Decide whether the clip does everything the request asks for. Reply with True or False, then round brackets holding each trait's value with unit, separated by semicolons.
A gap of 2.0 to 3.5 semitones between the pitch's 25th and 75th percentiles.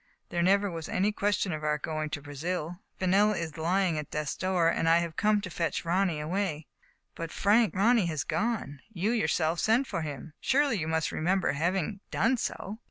False (4.3 semitones)